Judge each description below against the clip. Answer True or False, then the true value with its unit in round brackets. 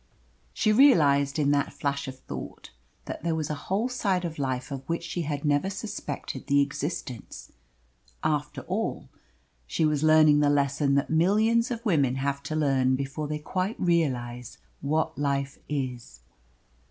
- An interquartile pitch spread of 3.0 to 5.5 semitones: True (3.3 semitones)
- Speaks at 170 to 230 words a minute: False (155 wpm)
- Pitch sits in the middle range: True (145 Hz)